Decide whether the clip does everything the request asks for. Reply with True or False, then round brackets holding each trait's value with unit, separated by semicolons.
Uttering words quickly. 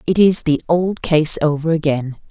False (180 wpm)